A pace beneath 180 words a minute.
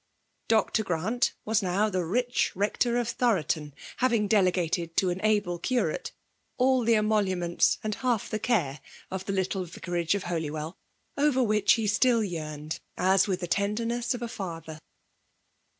Yes: average, 150 wpm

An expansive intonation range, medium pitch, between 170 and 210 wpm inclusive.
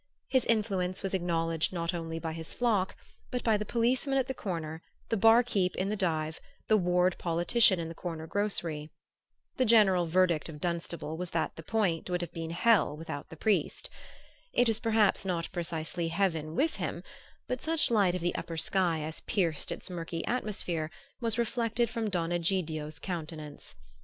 No: average, 4.6 semitones; medium, 180 Hz; average, 175 wpm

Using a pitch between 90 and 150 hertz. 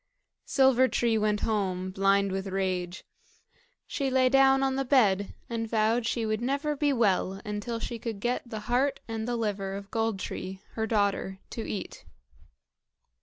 No: high, 220 Hz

